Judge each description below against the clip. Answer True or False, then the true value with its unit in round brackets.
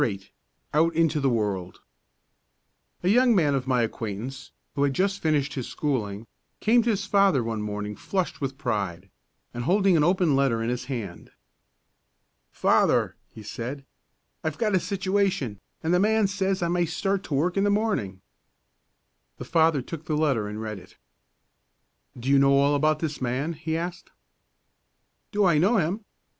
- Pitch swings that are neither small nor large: False (7.5 semitones)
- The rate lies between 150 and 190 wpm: True (170 wpm)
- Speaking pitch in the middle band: True (150 Hz)